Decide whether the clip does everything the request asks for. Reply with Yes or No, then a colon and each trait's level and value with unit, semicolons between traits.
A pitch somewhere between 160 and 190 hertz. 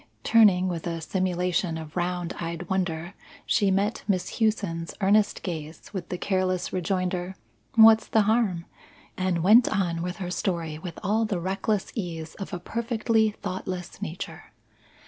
Yes: medium, 185 Hz